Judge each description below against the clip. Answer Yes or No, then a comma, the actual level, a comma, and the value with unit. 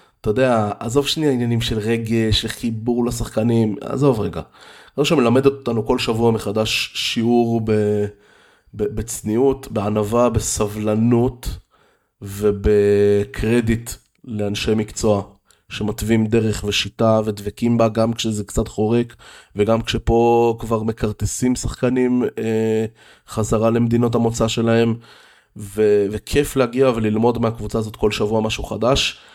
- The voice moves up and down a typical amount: No, narrow, 1.8 semitones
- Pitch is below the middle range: Yes, low, 115 Hz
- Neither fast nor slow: Yes, average, 110 wpm